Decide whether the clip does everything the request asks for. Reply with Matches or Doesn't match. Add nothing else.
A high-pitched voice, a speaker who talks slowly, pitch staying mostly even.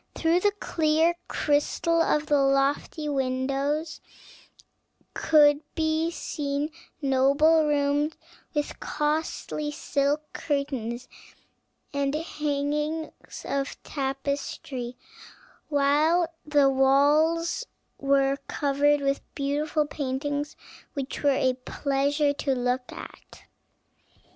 Matches